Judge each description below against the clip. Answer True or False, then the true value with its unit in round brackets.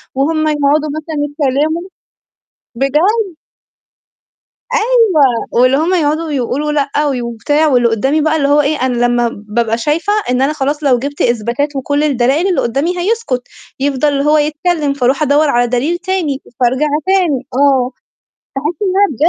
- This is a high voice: True (285 Hz)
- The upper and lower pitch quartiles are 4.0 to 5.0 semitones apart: False (3.3 semitones)